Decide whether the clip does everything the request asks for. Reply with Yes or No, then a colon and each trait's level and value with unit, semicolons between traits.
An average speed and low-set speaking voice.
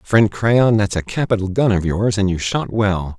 No: fast, 225 wpm; low, 100 Hz